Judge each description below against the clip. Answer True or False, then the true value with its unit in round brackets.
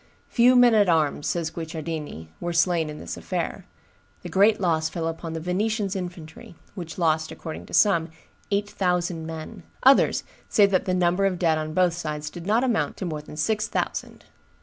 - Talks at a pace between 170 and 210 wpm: True (185 wpm)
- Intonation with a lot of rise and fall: False (3.7 semitones)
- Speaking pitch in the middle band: True (175 Hz)